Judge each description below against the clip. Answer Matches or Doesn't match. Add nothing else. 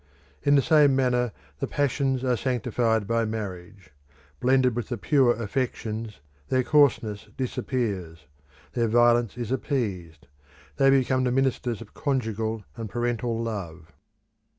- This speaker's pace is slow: Matches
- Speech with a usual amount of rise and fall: Matches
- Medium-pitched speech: Doesn't match